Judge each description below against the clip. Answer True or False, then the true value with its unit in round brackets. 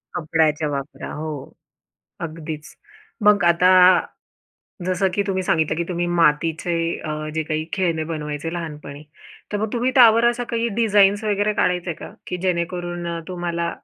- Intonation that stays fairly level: False (3.6 semitones)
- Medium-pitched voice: True (170 Hz)